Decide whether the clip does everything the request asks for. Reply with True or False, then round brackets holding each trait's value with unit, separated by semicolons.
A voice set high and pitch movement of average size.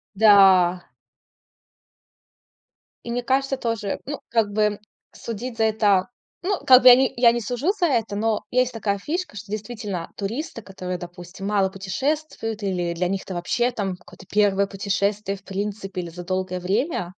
True (205 Hz; 3.8 semitones)